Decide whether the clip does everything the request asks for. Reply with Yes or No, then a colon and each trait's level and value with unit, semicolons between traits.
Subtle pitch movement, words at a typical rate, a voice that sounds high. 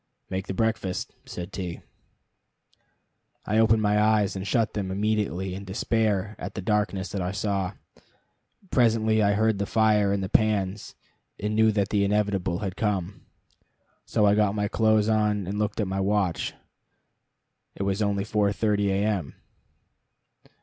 No: narrow, 1.8 semitones; average, 155 wpm; low, 105 Hz